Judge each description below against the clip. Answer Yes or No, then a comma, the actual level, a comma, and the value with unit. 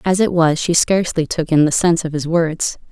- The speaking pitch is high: No, medium, 165 Hz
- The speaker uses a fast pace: Yes, fast, 245 wpm